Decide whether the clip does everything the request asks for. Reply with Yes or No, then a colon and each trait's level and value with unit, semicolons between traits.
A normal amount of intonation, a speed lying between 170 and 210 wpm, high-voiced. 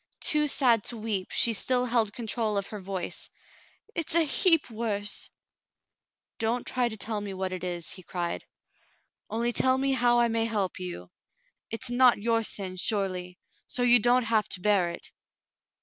Yes: average, 3.9 semitones; average, 180 wpm; high, 225 Hz